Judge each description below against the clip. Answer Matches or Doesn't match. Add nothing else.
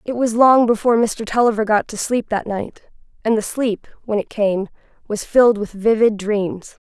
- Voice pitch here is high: Matches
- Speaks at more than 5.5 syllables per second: Doesn't match